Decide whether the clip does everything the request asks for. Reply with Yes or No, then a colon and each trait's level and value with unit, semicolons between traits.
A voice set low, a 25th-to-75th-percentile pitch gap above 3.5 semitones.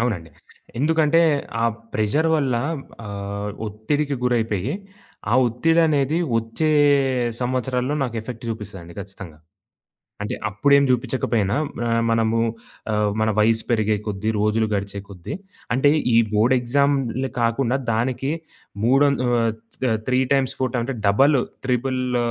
Yes: low, 120 Hz; average, 4.0 semitones